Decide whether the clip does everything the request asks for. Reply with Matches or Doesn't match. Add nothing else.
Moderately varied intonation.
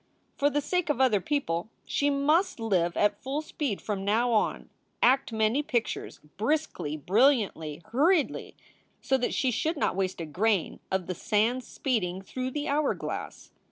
Doesn't match